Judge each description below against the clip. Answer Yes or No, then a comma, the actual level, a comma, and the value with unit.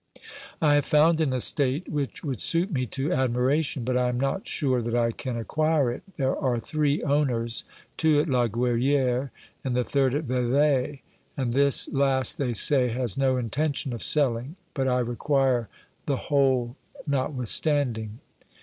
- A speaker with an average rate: Yes, average, 160 wpm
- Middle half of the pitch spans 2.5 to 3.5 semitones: Yes, average, 2.8 semitones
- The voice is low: Yes, low, 130 Hz